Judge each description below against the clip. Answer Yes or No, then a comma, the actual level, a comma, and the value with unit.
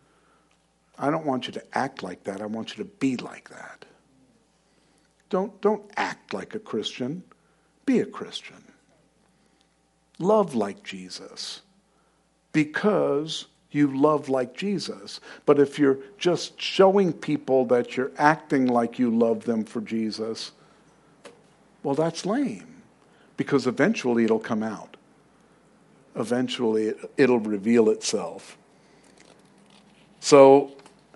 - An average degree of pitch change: No, wide, 5.8 semitones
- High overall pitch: No, low, 135 Hz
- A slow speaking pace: Yes, slow, 115 wpm